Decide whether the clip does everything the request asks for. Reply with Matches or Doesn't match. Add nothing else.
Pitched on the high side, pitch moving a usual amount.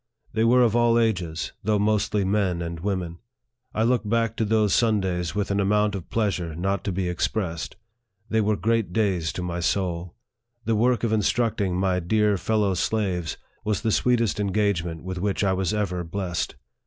Doesn't match